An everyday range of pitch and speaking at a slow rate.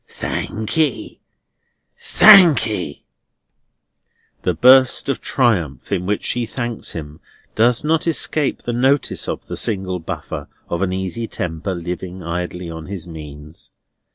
No: wide, 6.4 semitones; slow, 130 wpm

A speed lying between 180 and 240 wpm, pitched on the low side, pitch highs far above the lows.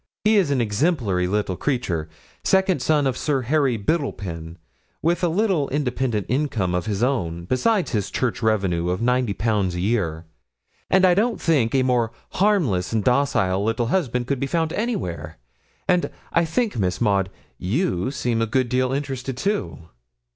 No: average, 165 wpm; low, 125 Hz; wide, 7.4 semitones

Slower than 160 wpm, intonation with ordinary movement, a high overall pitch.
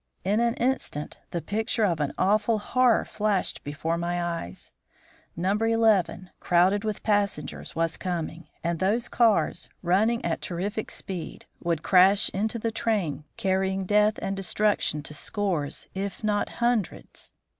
Yes: average, 140 wpm; average, 3.8 semitones; high, 195 Hz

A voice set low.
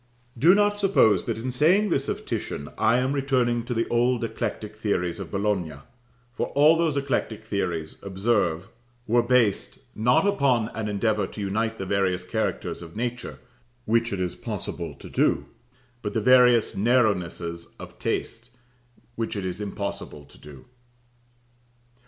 Yes: low, 110 Hz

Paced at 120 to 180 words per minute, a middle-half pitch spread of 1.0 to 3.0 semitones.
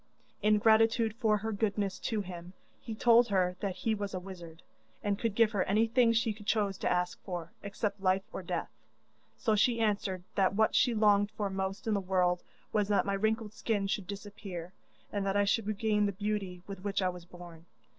No: average, 200 wpm; narrow, 2.4 semitones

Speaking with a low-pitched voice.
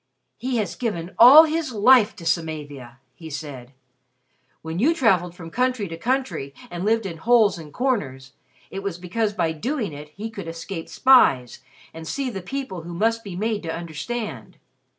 No: high, 195 Hz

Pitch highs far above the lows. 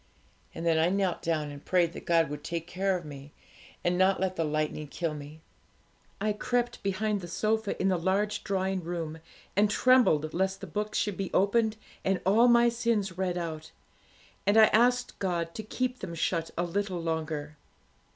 No: average, 4.1 semitones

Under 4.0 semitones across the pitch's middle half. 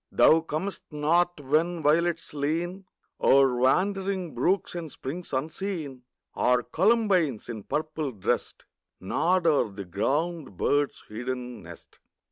No: average, 5.2 semitones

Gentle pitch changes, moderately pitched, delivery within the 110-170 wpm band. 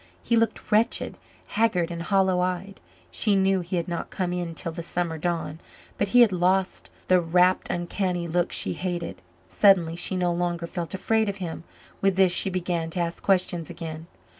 No: narrow, 2.0 semitones; medium, 180 Hz; average, 185 wpm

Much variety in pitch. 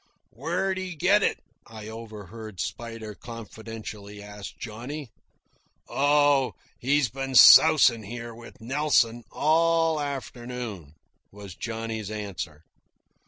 No: average, 4.8 semitones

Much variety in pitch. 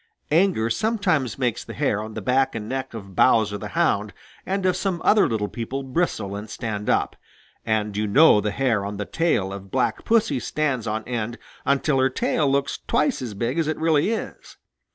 Yes: wide, 6.6 semitones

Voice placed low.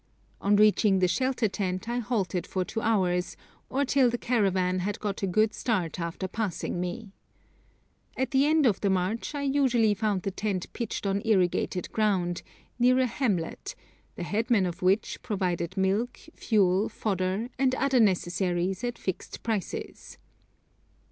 No: high, 205 Hz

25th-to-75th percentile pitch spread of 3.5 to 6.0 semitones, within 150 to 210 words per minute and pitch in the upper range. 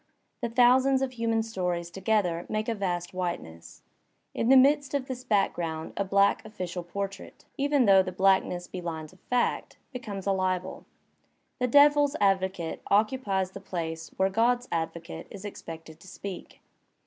Yes: average, 5.2 semitones; average, 160 wpm; high, 195 Hz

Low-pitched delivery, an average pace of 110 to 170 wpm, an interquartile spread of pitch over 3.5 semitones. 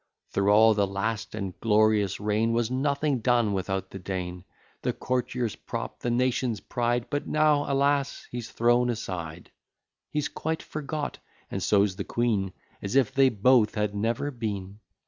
Yes: low, 115 Hz; average, 155 wpm; average, 4.1 semitones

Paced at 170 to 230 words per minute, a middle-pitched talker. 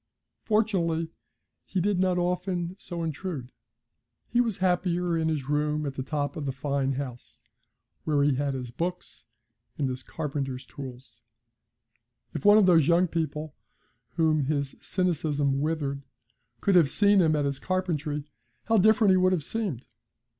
No: average, 155 wpm; medium, 160 Hz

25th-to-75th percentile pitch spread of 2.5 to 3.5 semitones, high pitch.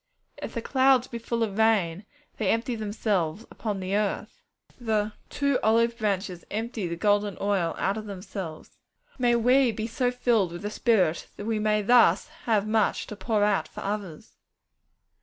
Yes: average, 2.8 semitones; high, 215 Hz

